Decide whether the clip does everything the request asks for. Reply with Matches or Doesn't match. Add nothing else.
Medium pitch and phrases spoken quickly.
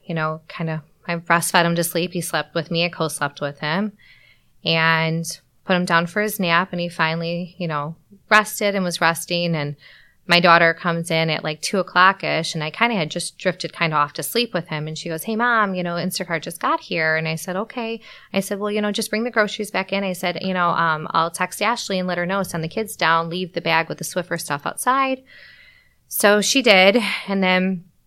Matches